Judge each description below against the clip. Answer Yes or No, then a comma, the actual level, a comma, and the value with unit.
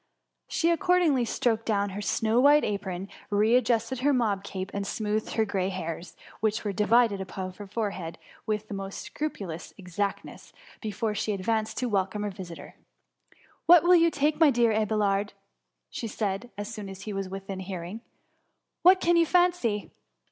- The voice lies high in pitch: Yes, high, 210 Hz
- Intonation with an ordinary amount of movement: Yes, average, 3.7 semitones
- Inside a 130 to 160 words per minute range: No, average, 175 wpm